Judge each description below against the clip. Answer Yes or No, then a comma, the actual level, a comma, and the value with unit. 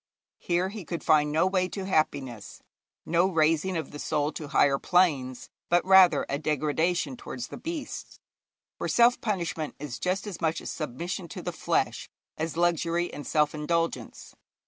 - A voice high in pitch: No, medium, 165 Hz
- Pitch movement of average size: Yes, average, 3.5 semitones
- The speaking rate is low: No, average, 165 wpm